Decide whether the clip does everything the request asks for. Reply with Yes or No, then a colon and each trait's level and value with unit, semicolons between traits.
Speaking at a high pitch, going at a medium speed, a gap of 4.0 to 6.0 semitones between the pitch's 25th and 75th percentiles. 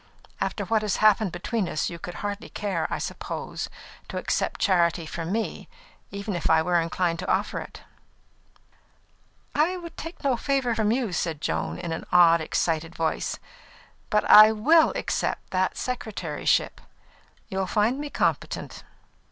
Yes: high, 195 Hz; average, 150 wpm; average, 5.1 semitones